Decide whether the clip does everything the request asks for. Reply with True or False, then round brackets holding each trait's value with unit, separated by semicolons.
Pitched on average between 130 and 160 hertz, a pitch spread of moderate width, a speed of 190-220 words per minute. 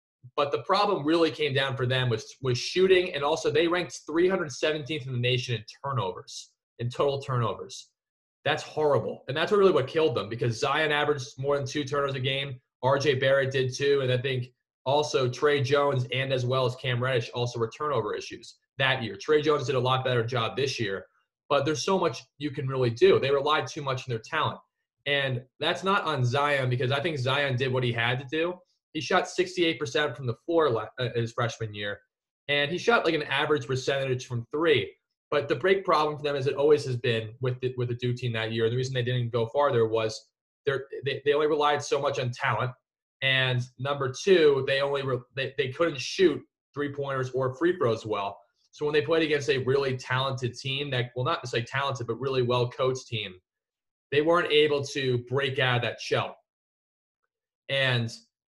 True (135 Hz; 3.3 semitones; 205 wpm)